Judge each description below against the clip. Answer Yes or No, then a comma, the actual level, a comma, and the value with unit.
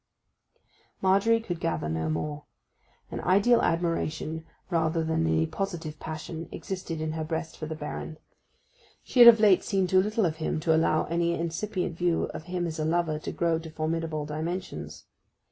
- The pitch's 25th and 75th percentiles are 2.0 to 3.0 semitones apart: Yes, narrow, 2.5 semitones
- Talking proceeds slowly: No, average, 170 wpm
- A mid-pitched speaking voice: Yes, medium, 165 Hz